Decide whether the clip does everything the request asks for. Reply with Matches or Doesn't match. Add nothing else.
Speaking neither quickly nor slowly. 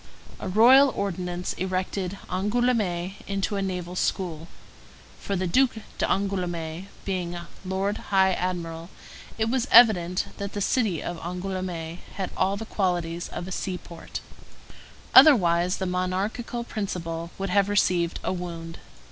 Doesn't match